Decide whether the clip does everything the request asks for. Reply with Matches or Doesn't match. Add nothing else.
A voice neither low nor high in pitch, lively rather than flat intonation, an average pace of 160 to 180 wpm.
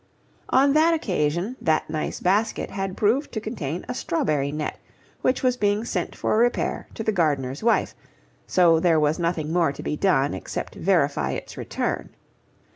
Matches